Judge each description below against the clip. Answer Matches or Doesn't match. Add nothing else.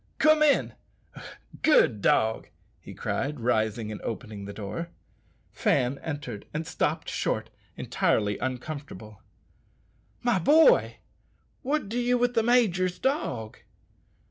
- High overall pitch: Doesn't match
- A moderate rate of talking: Doesn't match